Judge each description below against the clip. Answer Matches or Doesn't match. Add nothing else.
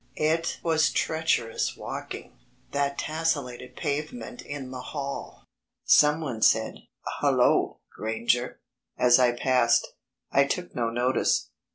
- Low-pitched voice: Matches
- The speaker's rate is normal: Doesn't match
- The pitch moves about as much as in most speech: Matches